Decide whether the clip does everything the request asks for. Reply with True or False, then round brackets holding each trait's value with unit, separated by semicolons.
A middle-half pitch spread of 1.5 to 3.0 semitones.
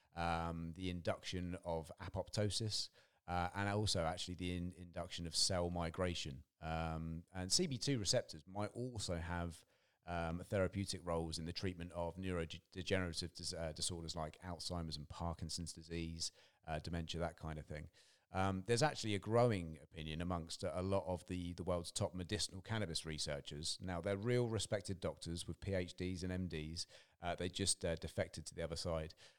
True (2.4 semitones)